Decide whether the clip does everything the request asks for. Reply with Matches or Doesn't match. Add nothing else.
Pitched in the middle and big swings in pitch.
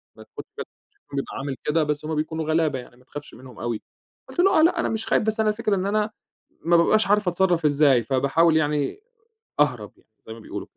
Matches